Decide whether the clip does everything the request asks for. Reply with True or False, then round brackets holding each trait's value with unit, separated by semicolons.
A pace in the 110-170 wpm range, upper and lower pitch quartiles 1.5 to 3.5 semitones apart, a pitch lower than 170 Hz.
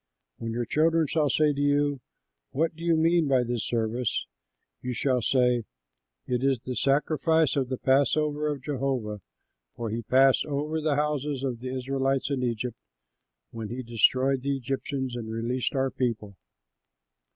True (160 wpm; 3.0 semitones; 135 Hz)